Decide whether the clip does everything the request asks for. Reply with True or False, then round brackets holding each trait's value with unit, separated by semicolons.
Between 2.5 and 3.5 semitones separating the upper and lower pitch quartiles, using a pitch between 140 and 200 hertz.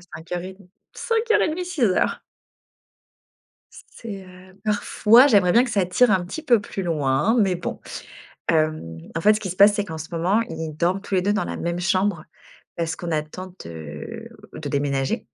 False (4.3 semitones; 185 Hz)